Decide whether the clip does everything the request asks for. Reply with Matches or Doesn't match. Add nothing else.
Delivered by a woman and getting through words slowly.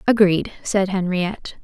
Matches